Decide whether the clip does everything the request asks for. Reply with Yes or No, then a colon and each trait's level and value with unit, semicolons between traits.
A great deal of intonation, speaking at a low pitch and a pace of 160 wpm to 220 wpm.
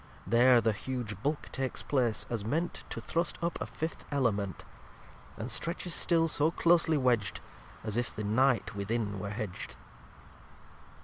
No: wide, 6.1 semitones; low, 120 Hz; average, 145 wpm